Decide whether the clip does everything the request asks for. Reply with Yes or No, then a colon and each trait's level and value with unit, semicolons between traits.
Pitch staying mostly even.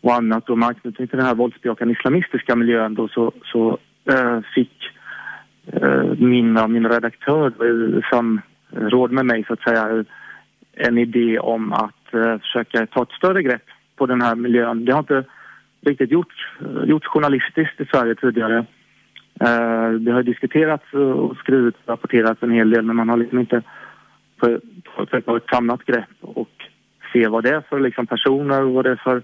Yes: narrow, 2.1 semitones